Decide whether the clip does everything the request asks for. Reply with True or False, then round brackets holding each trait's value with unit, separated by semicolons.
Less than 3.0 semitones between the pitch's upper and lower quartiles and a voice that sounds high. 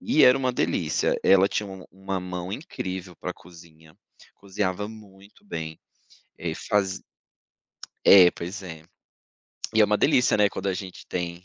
False (2.6 semitones; 95 Hz)